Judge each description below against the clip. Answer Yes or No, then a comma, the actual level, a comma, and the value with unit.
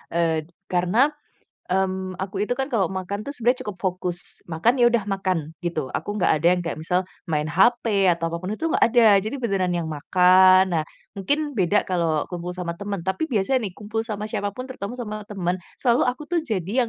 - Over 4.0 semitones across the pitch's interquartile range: Yes, average, 4.5 semitones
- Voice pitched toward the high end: Yes, high, 195 Hz